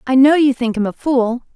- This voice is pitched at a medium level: No, very high, 255 Hz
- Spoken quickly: Yes, fast, 270 wpm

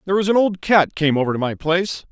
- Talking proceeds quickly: Yes, fast, 285 wpm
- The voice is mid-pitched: Yes, medium, 175 Hz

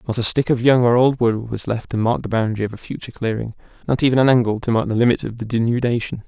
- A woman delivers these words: No, male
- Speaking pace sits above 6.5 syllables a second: Yes, 6.9 syllables/s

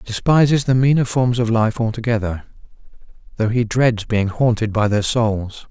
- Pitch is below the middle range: Yes, low, 115 Hz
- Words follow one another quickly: No, average, 160 wpm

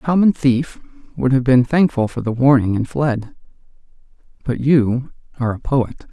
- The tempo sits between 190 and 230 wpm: No, average, 165 wpm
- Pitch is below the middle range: Yes, low, 130 Hz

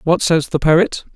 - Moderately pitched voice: Yes, medium, 160 Hz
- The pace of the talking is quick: Yes, fast, 210 wpm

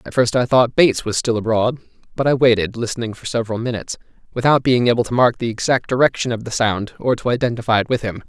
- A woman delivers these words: No, male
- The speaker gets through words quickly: Yes, fast, 230 wpm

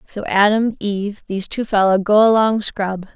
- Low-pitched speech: No, high, 205 Hz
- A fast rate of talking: No, average, 170 wpm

